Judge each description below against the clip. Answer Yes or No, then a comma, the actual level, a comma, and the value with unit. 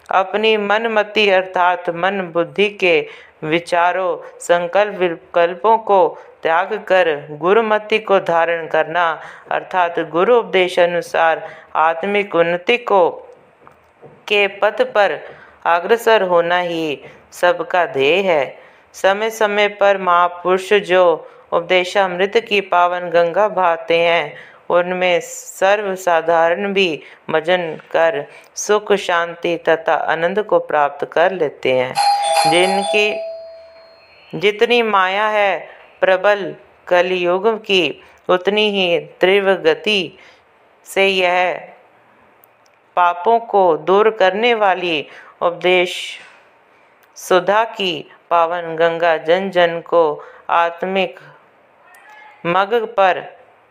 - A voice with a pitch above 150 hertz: Yes, medium, 185 Hz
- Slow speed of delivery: Yes, slow, 95 wpm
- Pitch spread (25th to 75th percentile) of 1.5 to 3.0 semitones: No, average, 3.6 semitones